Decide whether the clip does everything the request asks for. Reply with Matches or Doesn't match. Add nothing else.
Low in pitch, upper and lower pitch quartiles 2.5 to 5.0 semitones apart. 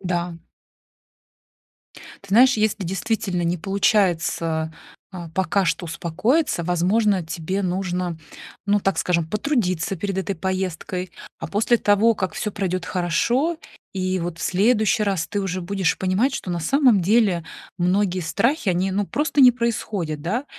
Doesn't match